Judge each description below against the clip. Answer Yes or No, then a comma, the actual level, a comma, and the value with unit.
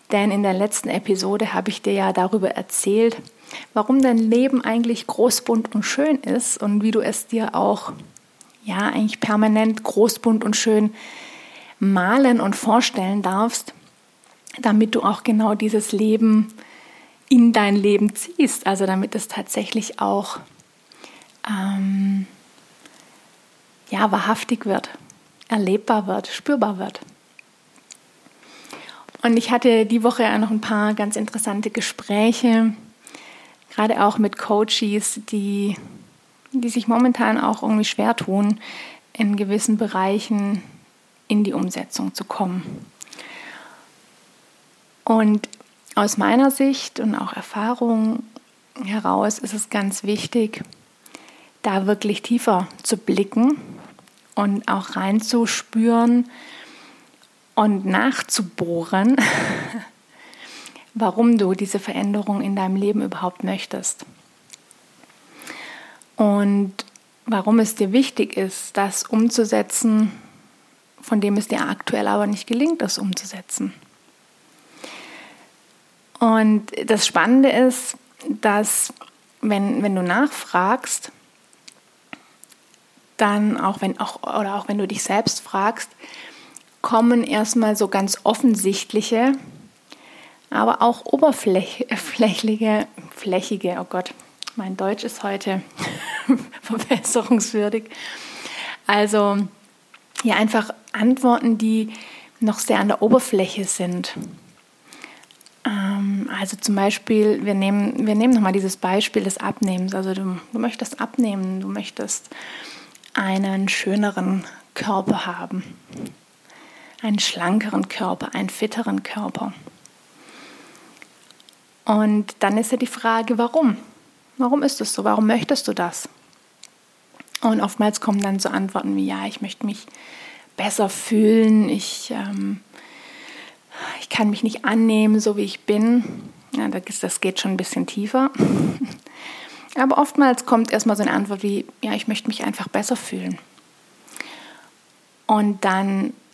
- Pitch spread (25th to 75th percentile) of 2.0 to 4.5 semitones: Yes, average, 2.8 semitones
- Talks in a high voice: Yes, high, 220 Hz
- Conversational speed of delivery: No, slow, 115 wpm